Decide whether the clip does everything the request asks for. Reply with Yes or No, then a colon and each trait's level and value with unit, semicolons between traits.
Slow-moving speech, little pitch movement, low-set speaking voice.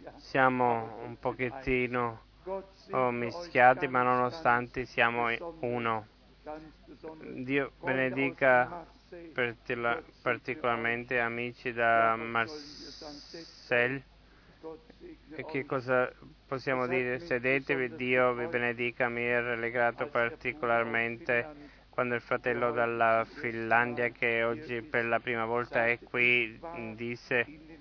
Yes: slow, 90 wpm; narrow, 2.2 semitones; low, 125 Hz